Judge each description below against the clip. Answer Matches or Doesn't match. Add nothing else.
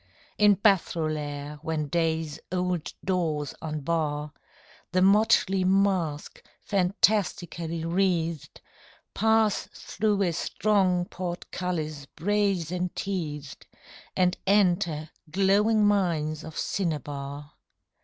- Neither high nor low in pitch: Matches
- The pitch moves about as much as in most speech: Matches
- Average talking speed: Doesn't match